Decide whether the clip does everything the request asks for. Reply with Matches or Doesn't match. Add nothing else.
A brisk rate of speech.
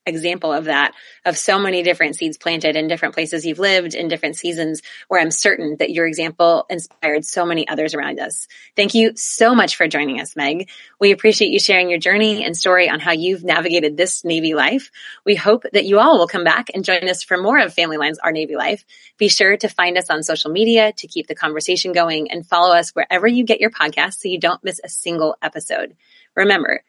Matches